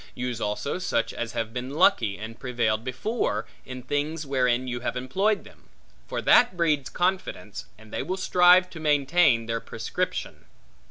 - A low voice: Yes, low, 130 Hz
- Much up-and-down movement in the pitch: Yes, wide, 6.2 semitones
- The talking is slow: No, average, 160 wpm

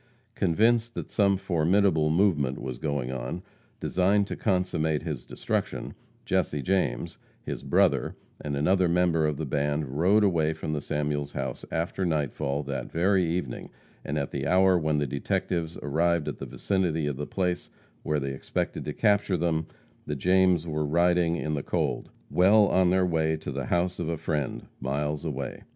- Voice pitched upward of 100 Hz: No, very low, 80 Hz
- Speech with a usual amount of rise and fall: Yes, average, 3.8 semitones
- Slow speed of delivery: No, average, 170 wpm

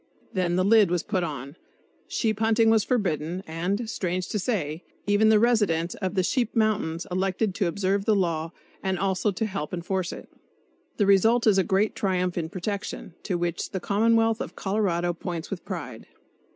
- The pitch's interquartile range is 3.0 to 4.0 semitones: Yes, average, 3.6 semitones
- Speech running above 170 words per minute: Yes, average, 180 wpm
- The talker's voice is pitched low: No, high, 190 Hz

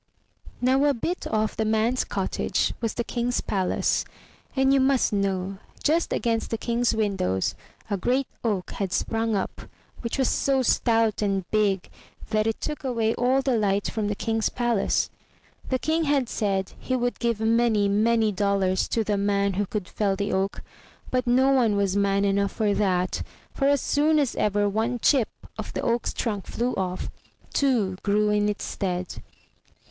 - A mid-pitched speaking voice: No, high, 220 Hz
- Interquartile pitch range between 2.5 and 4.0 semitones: Yes, average, 3.6 semitones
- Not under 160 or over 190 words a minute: Yes, average, 175 wpm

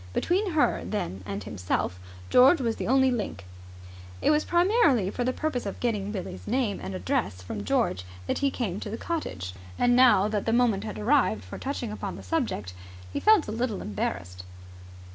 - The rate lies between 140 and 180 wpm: No, average, 190 wpm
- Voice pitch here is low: No, high, 225 Hz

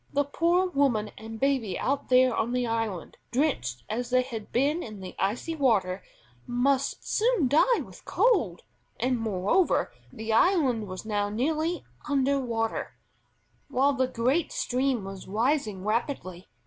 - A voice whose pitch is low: No, very high, 250 Hz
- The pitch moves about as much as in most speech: Yes, average, 4.6 semitones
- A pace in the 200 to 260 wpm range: No, average, 145 wpm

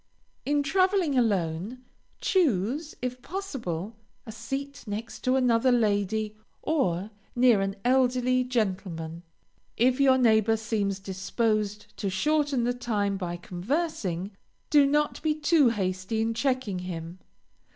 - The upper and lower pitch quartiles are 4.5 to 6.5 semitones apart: Yes, average, 5.2 semitones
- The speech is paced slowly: Yes, slow, 120 wpm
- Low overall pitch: No, high, 230 Hz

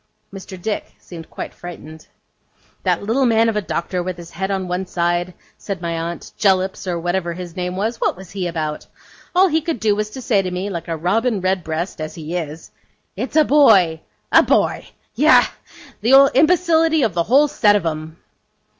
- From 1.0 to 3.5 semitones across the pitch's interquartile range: No, average, 4.5 semitones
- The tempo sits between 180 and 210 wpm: Yes, average, 190 wpm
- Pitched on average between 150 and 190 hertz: Yes, medium, 185 Hz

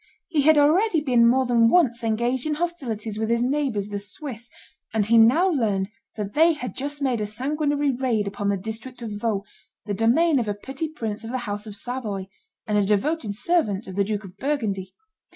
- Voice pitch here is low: No, high, 235 Hz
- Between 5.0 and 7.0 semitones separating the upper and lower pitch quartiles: Yes, wide, 5.5 semitones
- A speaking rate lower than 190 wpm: No, fast, 205 wpm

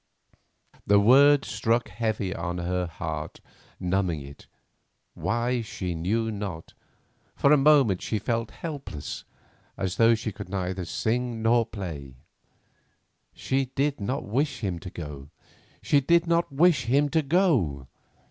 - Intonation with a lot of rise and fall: Yes, wide, 6.9 semitones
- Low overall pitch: Yes, low, 110 Hz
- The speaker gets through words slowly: Yes, slow, 130 wpm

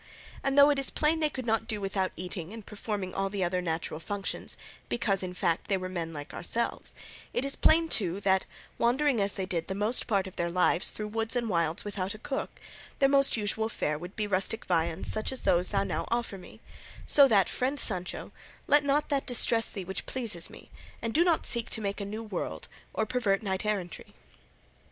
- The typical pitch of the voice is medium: No, high, 205 Hz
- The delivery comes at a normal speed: No, fast, 215 wpm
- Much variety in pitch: No, average, 4.4 semitones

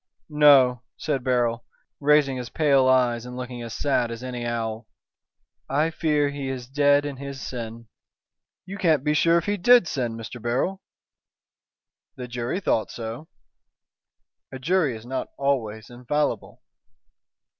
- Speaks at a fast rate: No, average, 145 wpm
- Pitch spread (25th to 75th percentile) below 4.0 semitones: Yes, average, 3.6 semitones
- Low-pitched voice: Yes, low, 130 Hz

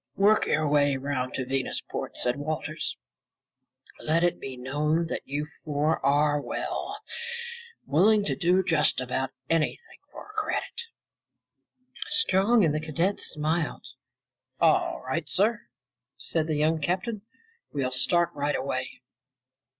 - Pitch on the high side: No, medium, 155 Hz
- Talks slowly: Yes, slow, 125 wpm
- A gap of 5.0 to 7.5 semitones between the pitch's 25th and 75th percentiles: No, average, 3.7 semitones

